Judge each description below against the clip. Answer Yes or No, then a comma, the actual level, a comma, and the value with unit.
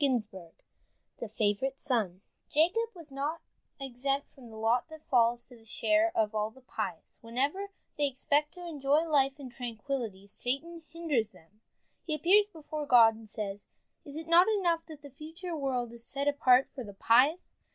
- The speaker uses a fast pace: No, average, 175 wpm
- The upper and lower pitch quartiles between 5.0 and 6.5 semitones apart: Yes, wide, 5.5 semitones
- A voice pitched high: Yes, very high, 270 Hz